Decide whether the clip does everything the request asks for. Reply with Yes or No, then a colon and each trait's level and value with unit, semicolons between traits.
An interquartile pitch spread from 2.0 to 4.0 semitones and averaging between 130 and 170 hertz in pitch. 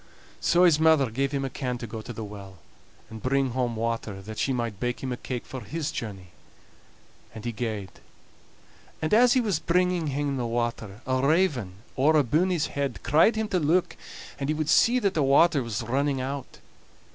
No: average, 5.2 semitones; low, 135 Hz